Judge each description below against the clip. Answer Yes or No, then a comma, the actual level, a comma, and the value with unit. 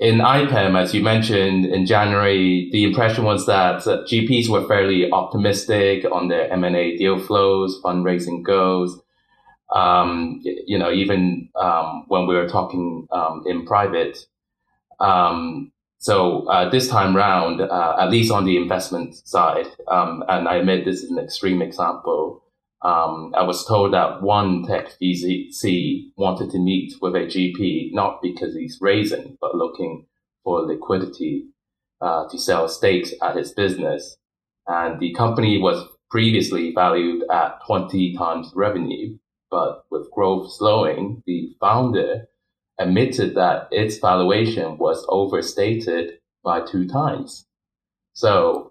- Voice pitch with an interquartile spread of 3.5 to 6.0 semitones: No, average, 3.0 semitones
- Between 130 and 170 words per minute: Yes, slow, 135 wpm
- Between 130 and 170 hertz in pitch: No, very low, 95 Hz